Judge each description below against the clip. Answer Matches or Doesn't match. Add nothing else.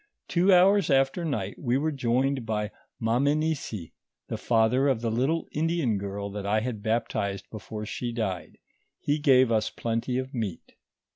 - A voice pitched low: Matches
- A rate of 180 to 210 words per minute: Doesn't match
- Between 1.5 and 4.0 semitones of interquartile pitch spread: Doesn't match